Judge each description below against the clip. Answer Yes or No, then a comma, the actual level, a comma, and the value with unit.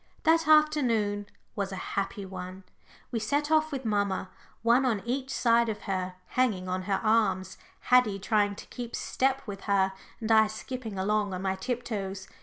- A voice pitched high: Yes, high, 215 Hz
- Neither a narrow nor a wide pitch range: Yes, average, 4.4 semitones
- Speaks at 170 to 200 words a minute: Yes, average, 175 wpm